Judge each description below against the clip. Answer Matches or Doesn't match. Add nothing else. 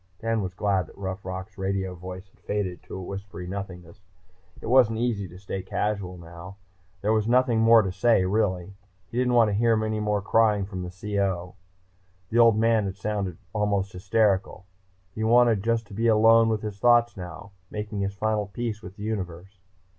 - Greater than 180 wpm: Matches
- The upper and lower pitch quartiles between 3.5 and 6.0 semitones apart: Doesn't match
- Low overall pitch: Matches